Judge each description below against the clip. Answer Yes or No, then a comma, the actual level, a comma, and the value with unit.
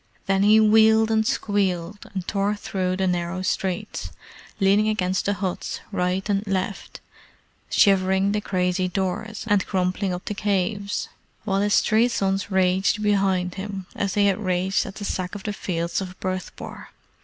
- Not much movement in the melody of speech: Yes, narrow, 1.9 semitones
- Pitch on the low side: No, high, 195 Hz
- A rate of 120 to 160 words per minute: Yes, average, 155 wpm